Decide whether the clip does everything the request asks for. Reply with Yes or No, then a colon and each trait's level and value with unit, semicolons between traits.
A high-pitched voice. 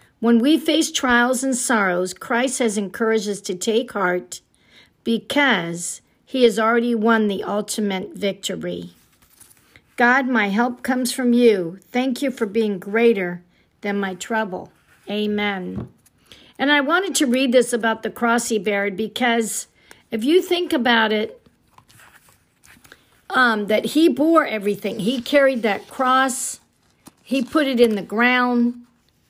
Yes: high, 230 Hz